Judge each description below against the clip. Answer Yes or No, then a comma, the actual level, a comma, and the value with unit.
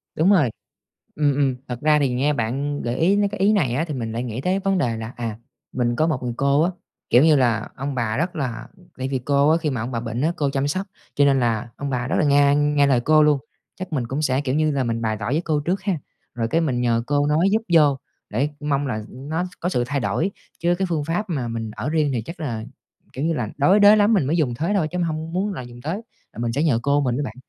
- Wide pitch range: No, average, 4.7 semitones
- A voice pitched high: No, medium, 145 Hz